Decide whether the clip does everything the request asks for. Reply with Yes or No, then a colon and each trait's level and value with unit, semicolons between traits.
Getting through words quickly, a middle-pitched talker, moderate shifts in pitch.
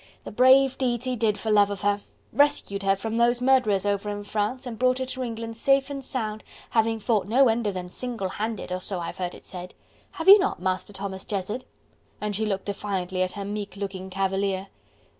No: fast, 210 wpm; high, 210 Hz; average, 4.0 semitones